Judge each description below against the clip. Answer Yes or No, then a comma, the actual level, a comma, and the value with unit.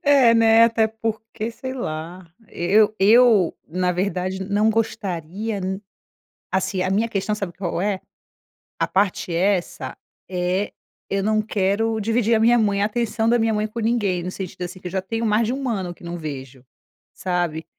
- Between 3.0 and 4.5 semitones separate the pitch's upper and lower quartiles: Yes, average, 3.6 semitones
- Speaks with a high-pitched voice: Yes, high, 200 Hz